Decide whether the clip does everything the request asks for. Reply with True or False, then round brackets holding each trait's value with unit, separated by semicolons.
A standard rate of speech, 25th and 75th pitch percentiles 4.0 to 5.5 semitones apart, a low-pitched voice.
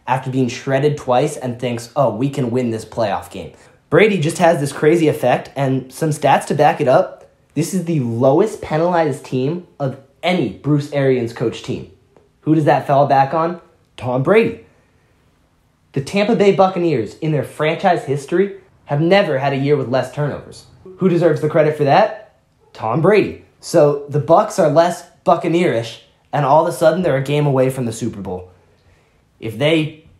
False (180 wpm; 4.3 semitones; 145 Hz)